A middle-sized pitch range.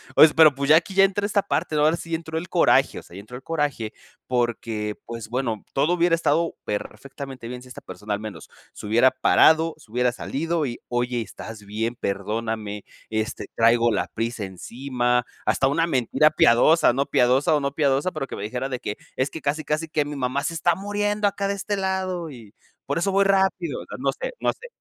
No: wide, 5.8 semitones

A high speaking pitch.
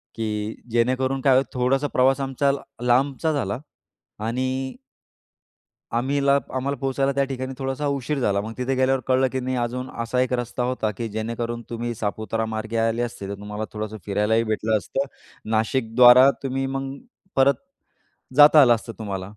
No: low, 125 Hz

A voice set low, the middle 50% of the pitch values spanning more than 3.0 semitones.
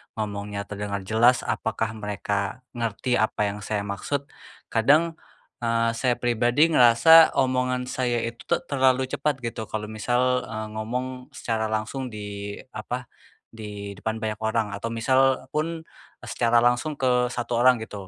No: low, 115 Hz; narrow, 2.6 semitones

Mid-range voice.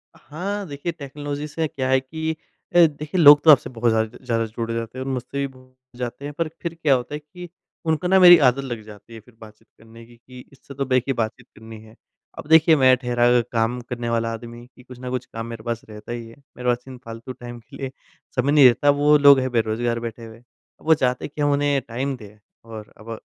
No: low, 125 Hz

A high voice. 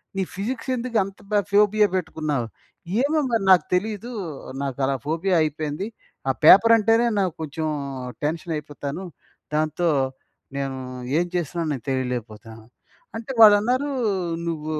No: medium, 170 Hz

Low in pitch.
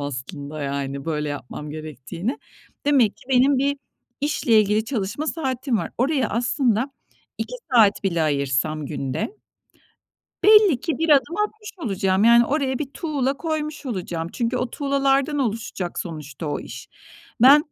No: high, 235 Hz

